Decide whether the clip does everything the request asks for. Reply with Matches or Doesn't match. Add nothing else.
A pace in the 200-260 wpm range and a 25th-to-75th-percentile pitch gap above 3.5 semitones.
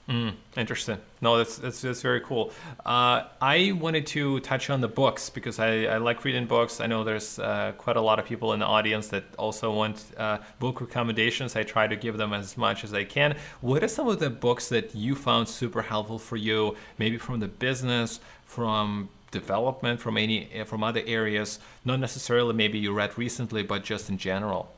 Doesn't match